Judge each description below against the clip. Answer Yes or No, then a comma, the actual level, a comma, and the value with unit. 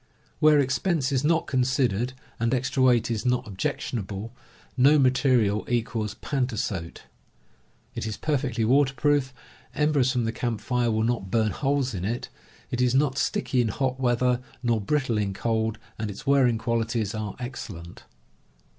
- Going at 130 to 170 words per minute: Yes, average, 160 wpm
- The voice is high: No, low, 120 Hz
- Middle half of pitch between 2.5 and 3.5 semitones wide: Yes, average, 3.2 semitones